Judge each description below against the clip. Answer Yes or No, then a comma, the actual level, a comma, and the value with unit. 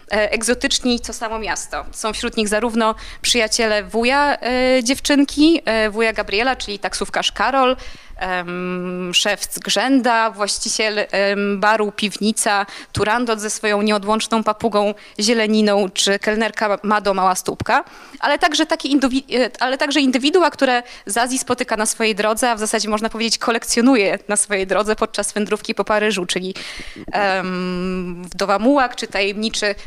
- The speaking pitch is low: No, high, 220 Hz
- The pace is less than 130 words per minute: No, average, 140 wpm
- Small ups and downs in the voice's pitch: No, average, 3.0 semitones